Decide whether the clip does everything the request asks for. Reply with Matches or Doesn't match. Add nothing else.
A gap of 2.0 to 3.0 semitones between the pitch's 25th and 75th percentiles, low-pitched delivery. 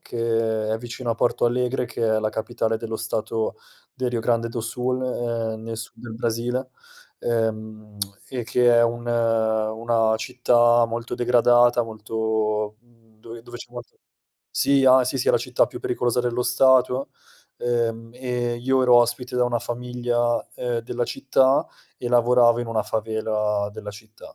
Doesn't match